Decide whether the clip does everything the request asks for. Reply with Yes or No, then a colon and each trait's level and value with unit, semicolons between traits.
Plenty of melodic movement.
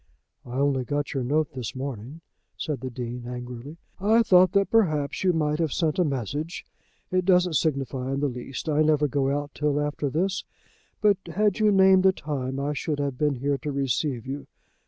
No: average, 3.9 semitones